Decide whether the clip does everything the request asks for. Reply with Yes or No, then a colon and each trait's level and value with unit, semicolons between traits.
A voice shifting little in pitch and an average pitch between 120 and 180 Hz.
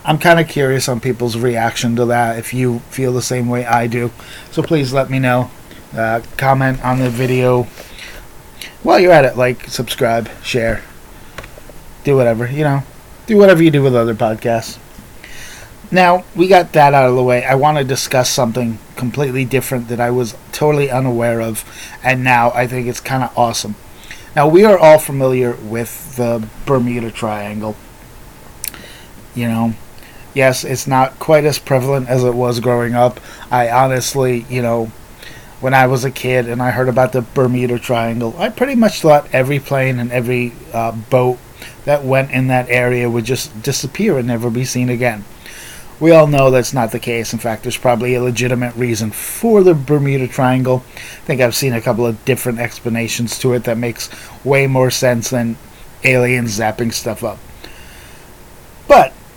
Yes: narrow, 2.0 semitones; low, 125 Hz